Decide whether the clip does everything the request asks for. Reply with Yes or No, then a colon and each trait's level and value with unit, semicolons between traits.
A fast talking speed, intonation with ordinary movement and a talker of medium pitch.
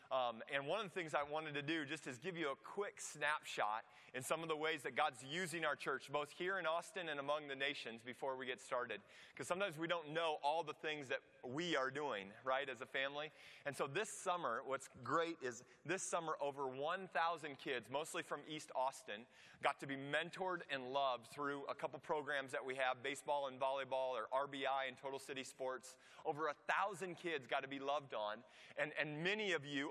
Yes: fast, 215 wpm; average, 3.4 semitones; medium, 145 Hz